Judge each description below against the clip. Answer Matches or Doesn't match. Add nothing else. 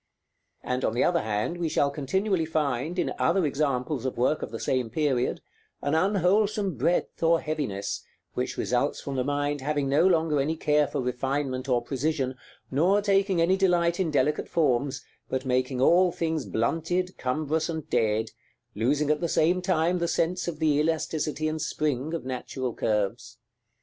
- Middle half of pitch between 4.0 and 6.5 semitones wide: Matches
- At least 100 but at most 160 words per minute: Doesn't match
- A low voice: Doesn't match